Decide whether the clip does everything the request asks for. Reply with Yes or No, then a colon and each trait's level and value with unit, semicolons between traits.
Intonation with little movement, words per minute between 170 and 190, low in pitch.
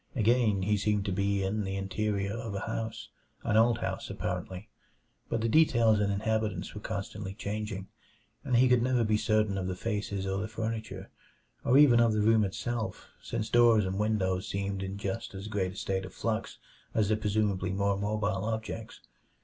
Yes: narrow, 2.2 semitones; average, 185 wpm; low, 105 Hz